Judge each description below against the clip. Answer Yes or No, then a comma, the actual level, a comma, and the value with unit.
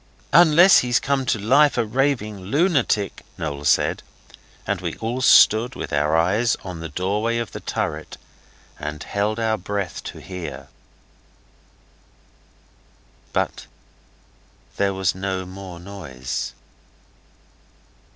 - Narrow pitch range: No, average, 5.3 semitones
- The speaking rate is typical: No, slow, 115 wpm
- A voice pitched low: Yes, low, 100 Hz